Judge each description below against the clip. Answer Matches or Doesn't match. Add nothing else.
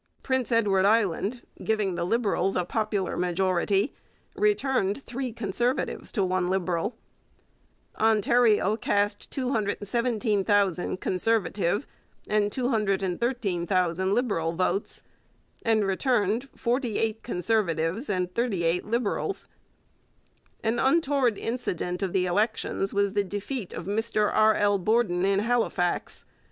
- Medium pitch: Doesn't match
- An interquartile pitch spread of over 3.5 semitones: Matches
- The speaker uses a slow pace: Matches